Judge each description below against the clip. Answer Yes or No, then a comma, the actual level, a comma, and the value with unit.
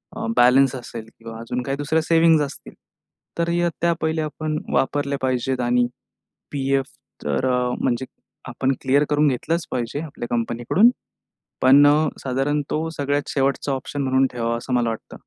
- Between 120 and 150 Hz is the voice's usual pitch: Yes, low, 135 Hz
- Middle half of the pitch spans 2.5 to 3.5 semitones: Yes, average, 3.1 semitones